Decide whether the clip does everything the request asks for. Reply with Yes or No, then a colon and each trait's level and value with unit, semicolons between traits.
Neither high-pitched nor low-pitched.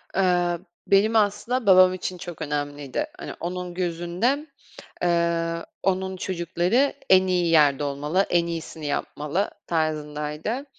Yes: medium, 175 Hz